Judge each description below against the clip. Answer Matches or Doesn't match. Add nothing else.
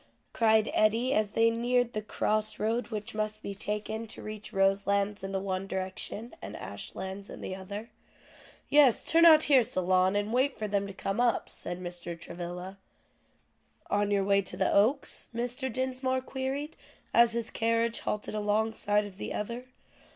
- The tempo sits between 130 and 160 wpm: Doesn't match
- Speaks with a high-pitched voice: Matches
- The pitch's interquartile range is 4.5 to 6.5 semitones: Doesn't match